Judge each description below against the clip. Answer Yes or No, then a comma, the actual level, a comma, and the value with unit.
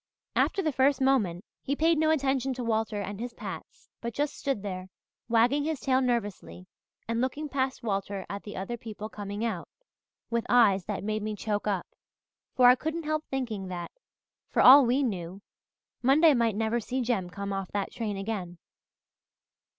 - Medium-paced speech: Yes, average, 175 wpm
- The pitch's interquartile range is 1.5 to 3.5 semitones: No, average, 4.8 semitones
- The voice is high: Yes, high, 230 Hz